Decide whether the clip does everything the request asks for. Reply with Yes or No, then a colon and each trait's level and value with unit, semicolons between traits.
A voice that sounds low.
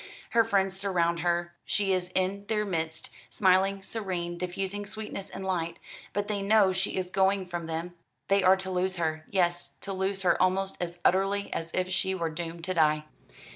No: medium, 185 Hz